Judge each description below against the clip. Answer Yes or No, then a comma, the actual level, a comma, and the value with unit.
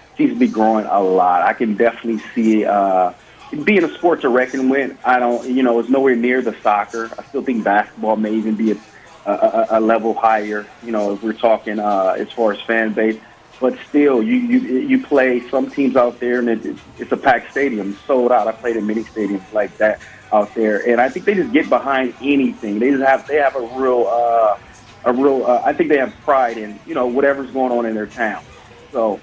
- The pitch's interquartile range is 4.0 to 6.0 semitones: No, average, 3.3 semitones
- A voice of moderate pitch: No, low, 120 Hz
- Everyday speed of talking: No, fast, 230 wpm